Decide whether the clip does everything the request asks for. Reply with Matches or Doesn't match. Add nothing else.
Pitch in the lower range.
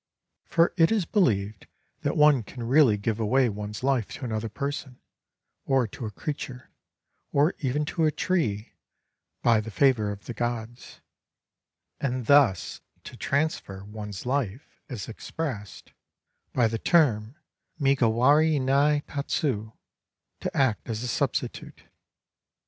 Matches